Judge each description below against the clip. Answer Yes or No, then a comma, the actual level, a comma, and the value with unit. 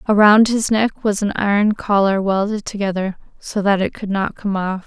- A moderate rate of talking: Yes, average, 195 wpm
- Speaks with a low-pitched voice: No, high, 205 Hz